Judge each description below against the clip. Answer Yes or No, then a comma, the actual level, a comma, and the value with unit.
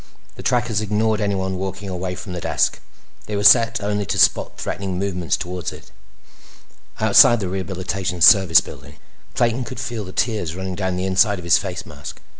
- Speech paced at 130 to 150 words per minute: No, average, 180 wpm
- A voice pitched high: No, very low, 95 Hz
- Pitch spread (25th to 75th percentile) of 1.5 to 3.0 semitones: Yes, narrow, 2.5 semitones